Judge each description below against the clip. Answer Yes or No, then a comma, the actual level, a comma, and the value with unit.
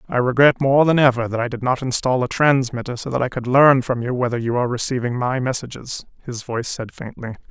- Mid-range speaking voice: No, low, 125 Hz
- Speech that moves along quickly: Yes, fast, 230 wpm